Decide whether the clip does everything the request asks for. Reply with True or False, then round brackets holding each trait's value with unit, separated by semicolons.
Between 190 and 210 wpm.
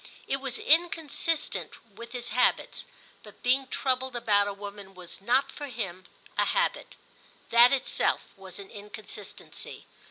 False (135 wpm)